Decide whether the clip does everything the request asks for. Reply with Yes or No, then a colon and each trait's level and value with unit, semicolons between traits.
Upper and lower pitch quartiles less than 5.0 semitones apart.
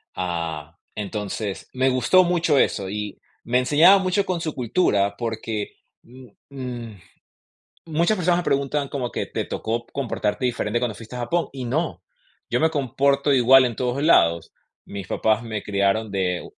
No: average, 5.3 semitones